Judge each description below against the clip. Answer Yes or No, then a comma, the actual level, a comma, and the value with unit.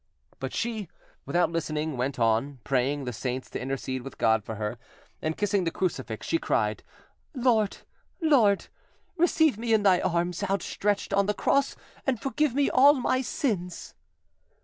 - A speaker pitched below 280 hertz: Yes, medium, 185 Hz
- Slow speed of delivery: No, average, 160 wpm